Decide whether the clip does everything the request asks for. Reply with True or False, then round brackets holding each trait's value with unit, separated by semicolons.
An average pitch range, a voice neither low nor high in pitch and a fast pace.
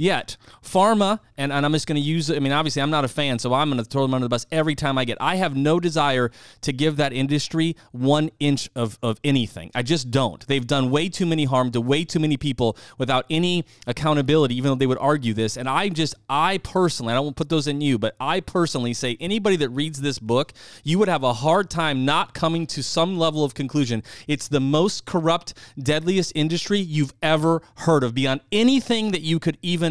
True (3.8 semitones; 145 Hz; 235 wpm)